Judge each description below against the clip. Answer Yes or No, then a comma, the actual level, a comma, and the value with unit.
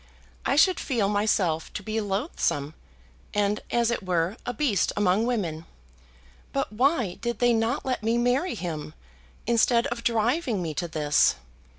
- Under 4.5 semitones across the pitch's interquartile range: No, average, 4.8 semitones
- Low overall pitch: No, high, 220 Hz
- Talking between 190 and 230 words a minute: No, average, 155 wpm